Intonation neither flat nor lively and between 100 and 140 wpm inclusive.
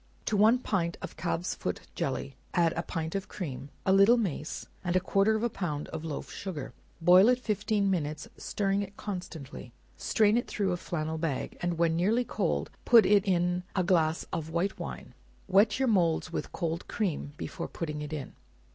No: average, 3.9 semitones; average, 185 wpm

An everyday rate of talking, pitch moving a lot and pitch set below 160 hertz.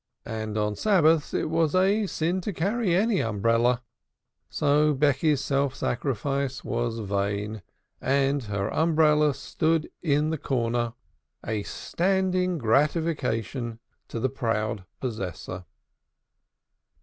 No: slow, 110 wpm; wide, 6.1 semitones; medium, 140 Hz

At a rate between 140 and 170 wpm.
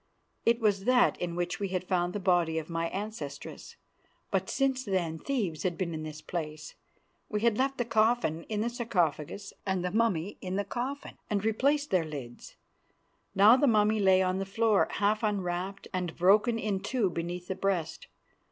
No: average, 180 wpm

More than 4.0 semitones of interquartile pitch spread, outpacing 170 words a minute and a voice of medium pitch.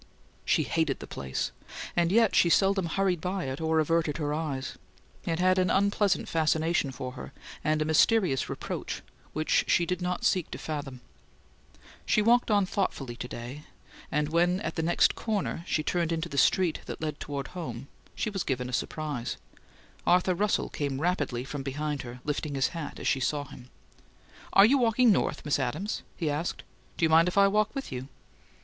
Yes: average, 4.5 semitones; average, 185 wpm; medium, 160 Hz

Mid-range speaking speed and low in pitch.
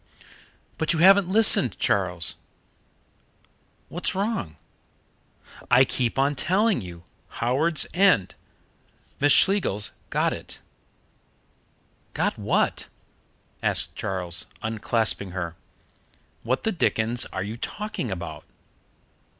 No: slow, 100 wpm; low, 120 Hz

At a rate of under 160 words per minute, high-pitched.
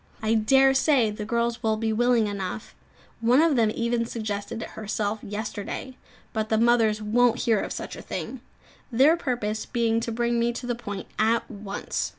No: average, 180 wpm; high, 230 Hz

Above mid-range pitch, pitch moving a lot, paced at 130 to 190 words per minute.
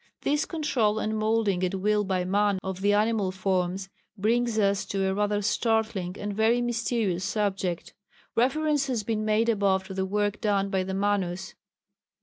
No: high, 205 Hz; narrow, 2.6 semitones; average, 165 wpm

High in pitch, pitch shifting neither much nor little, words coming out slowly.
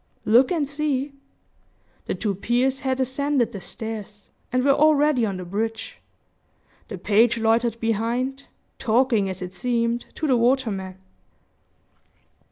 Yes: high, 235 Hz; average, 3.5 semitones; slow, 130 wpm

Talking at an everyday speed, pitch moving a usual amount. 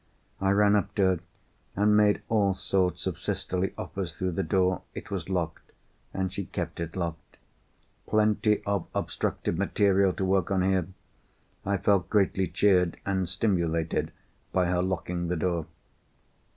No: average, 150 wpm; narrow, 2.0 semitones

